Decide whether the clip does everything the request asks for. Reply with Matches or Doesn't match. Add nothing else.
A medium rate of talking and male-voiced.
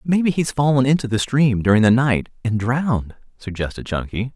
Matches